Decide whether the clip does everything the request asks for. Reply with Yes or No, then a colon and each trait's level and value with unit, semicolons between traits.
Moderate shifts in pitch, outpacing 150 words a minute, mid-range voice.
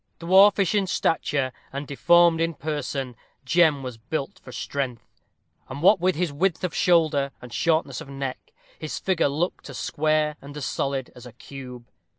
Yes: average, 3.9 semitones; average, 165 wpm; medium, 145 Hz